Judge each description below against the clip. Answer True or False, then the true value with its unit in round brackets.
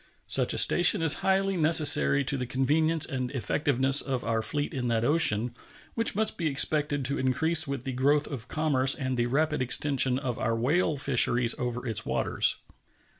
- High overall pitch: False (140 Hz)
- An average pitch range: True (3.7 semitones)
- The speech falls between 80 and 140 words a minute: False (175 wpm)